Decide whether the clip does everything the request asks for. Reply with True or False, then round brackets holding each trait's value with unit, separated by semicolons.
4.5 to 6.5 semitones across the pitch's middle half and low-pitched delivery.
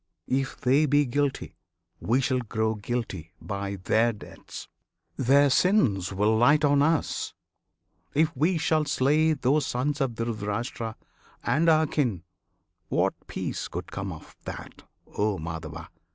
True (5.5 semitones; 125 Hz)